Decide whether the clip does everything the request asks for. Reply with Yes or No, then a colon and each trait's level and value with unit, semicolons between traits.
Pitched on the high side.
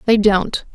Yes: high, 205 Hz